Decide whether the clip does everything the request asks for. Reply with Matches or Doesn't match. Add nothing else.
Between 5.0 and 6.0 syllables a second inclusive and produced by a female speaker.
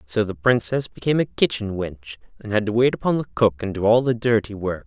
Doesn't match